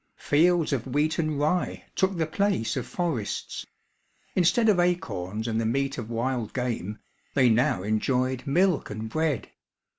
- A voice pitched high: No, low, 135 Hz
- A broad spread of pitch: Yes, wide, 6.5 semitones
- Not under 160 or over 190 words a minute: No, average, 150 wpm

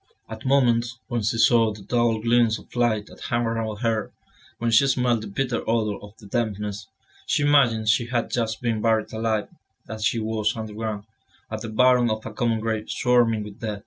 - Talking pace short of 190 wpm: No, average, 195 wpm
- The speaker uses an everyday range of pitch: No, narrow, 1.6 semitones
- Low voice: Yes, low, 115 Hz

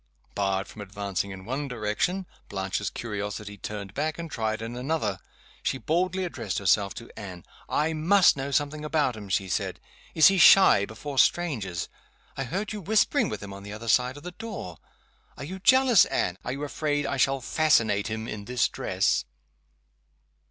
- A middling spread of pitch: No, wide, 7.4 semitones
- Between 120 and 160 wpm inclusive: No, average, 175 wpm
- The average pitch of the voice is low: Yes, low, 125 Hz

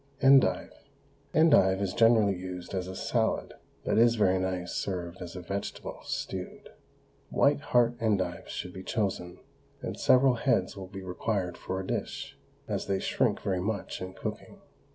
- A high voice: No, very low, 95 Hz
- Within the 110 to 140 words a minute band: No, average, 155 wpm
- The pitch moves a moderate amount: Yes, average, 3.5 semitones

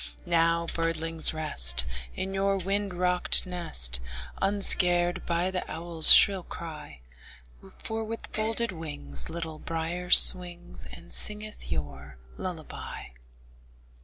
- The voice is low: No, medium, 170 Hz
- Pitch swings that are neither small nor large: Yes, average, 3.1 semitones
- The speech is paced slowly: Yes, slow, 105 wpm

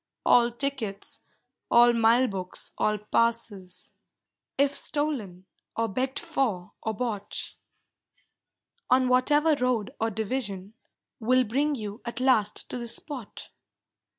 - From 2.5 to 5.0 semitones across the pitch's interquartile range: Yes, average, 3.7 semitones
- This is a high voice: Yes, high, 235 Hz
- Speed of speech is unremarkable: No, slow, 115 wpm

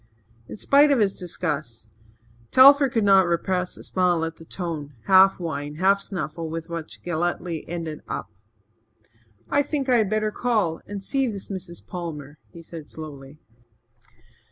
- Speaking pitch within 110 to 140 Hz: No, medium, 175 Hz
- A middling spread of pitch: Yes, average, 4.1 semitones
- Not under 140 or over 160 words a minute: Yes, average, 155 wpm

